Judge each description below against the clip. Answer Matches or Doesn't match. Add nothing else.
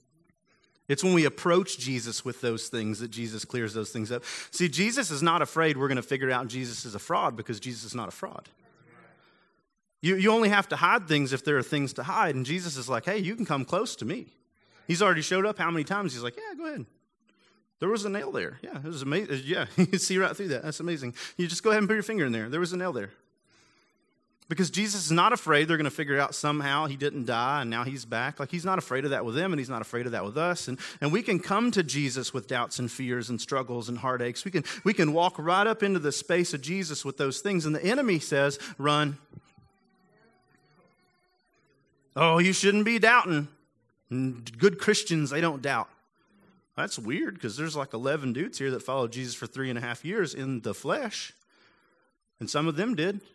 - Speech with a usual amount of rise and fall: Doesn't match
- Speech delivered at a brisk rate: Matches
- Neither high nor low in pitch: Matches